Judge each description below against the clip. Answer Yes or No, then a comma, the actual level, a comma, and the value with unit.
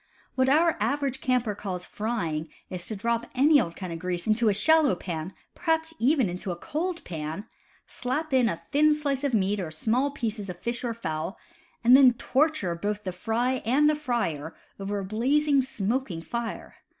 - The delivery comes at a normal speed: Yes, average, 185 wpm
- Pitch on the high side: Yes, high, 230 Hz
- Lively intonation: Yes, wide, 6.7 semitones